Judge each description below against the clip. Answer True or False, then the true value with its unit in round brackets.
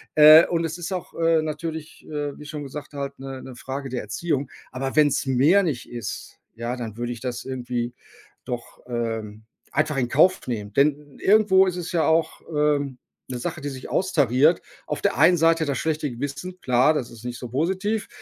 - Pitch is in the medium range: True (145 Hz)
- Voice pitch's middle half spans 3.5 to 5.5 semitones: True (4.5 semitones)